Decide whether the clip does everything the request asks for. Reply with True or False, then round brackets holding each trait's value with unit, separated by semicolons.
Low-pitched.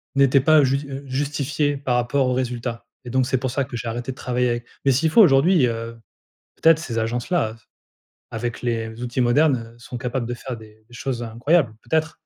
True (125 Hz)